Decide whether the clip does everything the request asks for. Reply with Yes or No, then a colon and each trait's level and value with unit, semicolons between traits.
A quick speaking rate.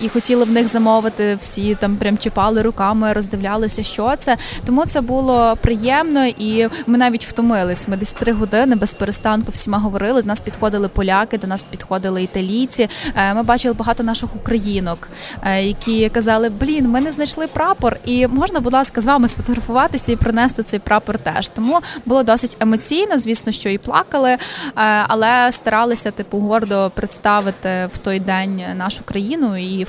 Yes: fast, 160 wpm